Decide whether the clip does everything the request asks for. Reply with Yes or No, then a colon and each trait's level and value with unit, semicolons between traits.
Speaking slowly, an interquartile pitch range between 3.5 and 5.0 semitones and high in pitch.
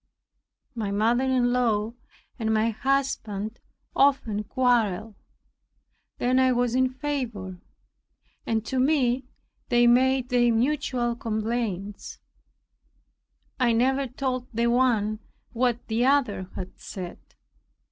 No: slow, 105 wpm; average, 2.8 semitones; high, 240 Hz